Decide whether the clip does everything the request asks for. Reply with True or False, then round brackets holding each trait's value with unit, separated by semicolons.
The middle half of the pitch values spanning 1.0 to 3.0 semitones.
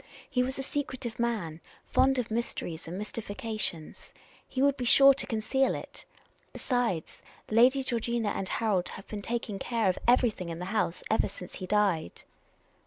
False (4.6 semitones)